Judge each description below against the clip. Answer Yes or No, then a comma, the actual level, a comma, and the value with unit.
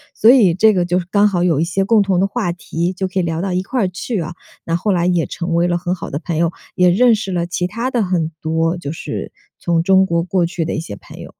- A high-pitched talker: No, medium, 180 Hz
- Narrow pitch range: Yes, narrow, 2.3 semitones